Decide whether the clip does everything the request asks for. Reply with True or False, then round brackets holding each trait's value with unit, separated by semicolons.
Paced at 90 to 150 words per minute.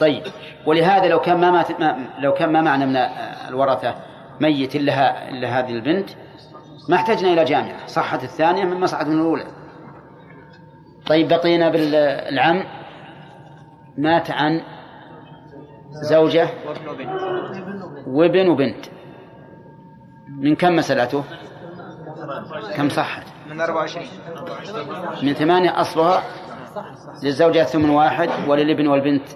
True (100 wpm)